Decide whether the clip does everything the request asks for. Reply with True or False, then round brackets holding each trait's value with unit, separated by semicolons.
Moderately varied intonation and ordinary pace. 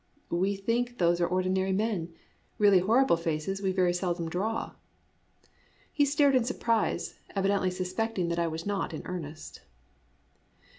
True (4.0 semitones; 145 wpm)